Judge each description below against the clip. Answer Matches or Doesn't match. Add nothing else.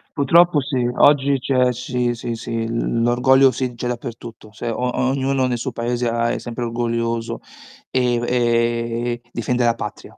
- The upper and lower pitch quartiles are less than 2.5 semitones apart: Matches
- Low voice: Matches